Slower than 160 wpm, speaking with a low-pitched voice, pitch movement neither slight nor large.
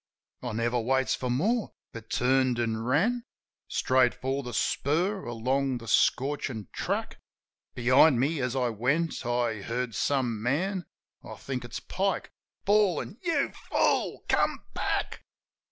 Yes: average, 140 wpm; low, 130 Hz; average, 4.9 semitones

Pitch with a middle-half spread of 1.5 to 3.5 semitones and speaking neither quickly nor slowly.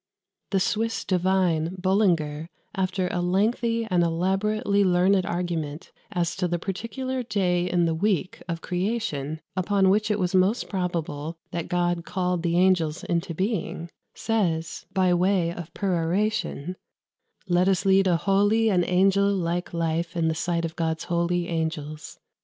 Yes: narrow, 2.6 semitones; average, 145 wpm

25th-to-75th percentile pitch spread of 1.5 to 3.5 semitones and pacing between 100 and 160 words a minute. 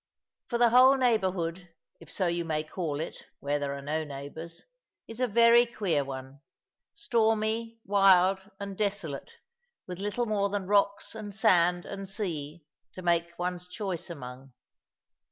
No: average, 4.8 semitones; average, 150 wpm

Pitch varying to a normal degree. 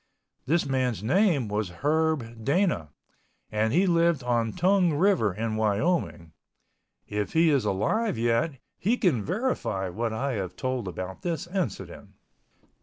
No: wide, 7.8 semitones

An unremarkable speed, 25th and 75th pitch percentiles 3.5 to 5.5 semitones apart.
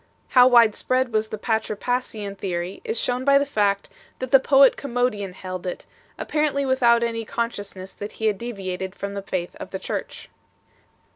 Yes: average, 160 wpm; average, 4.1 semitones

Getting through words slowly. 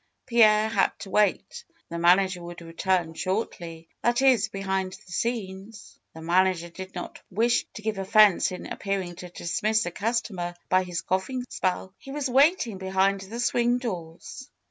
No: average, 170 wpm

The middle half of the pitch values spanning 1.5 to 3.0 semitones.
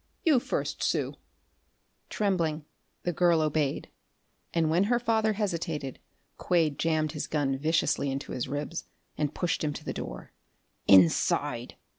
No: average, 3.4 semitones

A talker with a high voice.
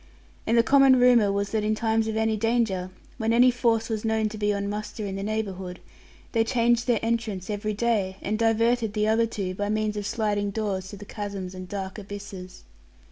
Yes: high, 215 Hz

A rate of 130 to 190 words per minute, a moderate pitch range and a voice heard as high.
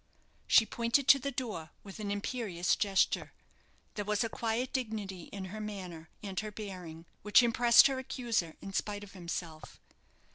Yes: average, 160 wpm; average, 3.7 semitones; high, 210 Hz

